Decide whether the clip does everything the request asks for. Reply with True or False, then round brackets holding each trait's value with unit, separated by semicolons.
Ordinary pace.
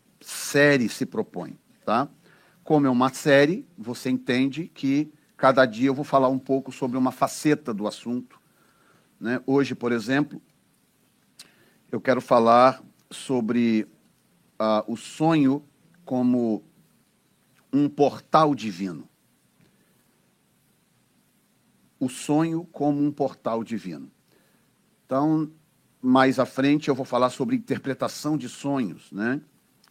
False (110 wpm)